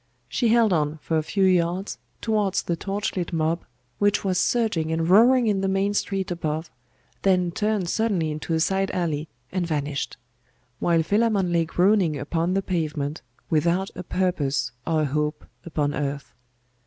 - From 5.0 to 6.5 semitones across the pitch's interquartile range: No, average, 3.7 semitones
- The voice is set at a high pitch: No, medium, 175 Hz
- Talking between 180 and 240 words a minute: No, average, 165 wpm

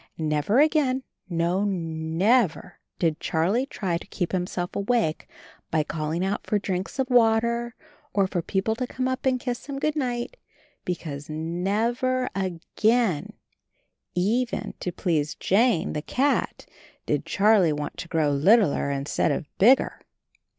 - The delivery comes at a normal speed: Yes, average, 145 wpm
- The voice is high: Yes, high, 195 Hz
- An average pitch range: No, wide, 6.5 semitones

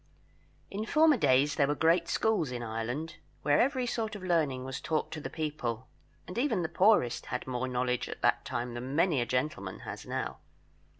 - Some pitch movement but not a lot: No, wide, 6.4 semitones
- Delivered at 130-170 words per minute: No, average, 190 wpm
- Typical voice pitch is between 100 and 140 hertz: No, medium, 150 Hz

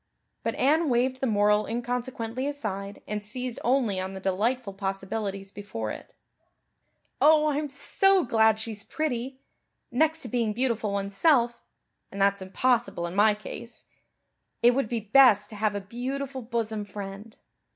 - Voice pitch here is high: Yes, high, 225 Hz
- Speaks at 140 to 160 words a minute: Yes, average, 145 wpm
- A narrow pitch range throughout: No, average, 4.1 semitones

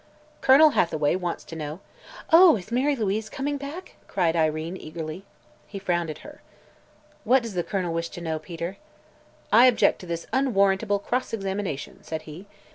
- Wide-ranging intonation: Yes, wide, 6.3 semitones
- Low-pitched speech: No, high, 190 Hz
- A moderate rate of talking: Yes, average, 170 wpm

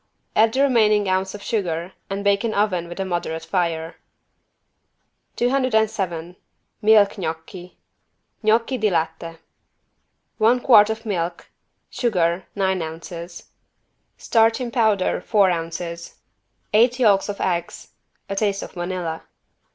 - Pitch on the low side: No, high, 195 Hz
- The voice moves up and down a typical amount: Yes, average, 4.2 semitones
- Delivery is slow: Yes, slow, 120 wpm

